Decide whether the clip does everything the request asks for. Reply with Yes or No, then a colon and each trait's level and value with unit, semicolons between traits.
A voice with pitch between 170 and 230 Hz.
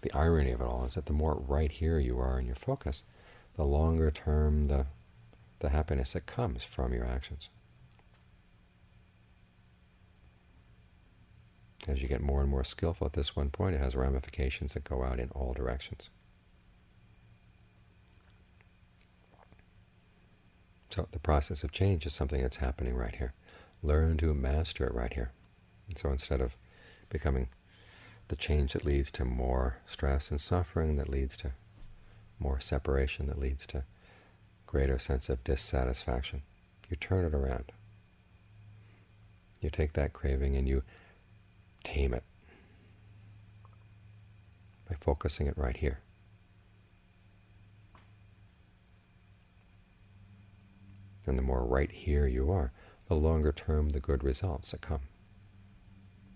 No: very low, 85 Hz